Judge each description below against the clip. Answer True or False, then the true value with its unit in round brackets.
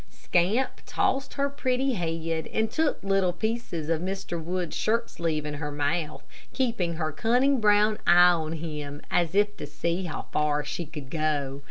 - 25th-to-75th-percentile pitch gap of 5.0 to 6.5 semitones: True (5.5 semitones)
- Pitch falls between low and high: True (175 Hz)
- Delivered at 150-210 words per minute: True (170 wpm)